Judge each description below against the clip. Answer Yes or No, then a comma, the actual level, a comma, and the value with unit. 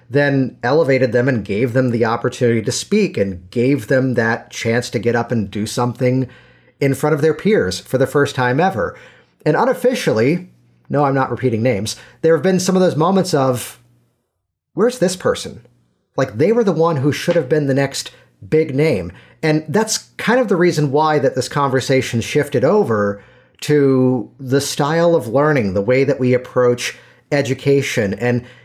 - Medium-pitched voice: No, low, 130 Hz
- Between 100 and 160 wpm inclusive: No, average, 180 wpm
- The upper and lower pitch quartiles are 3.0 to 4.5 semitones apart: Yes, average, 4.2 semitones